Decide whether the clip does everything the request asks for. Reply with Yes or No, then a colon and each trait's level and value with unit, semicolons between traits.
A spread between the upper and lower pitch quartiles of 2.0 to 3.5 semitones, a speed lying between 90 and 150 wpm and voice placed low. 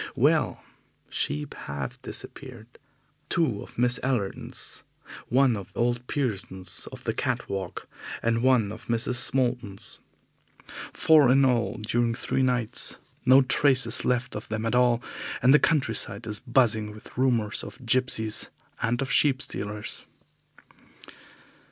Yes: average, 3.0 semitones; slow, 135 wpm; low, 120 Hz